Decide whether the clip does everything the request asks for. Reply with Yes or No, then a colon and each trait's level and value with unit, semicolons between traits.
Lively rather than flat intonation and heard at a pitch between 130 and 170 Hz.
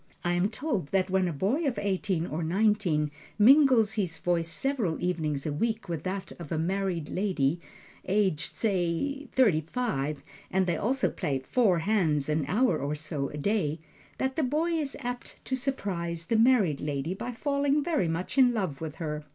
No: wide, 7.0 semitones; medium, 185 Hz